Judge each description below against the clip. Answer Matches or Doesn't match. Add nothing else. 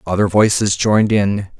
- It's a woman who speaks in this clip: Doesn't match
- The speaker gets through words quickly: Doesn't match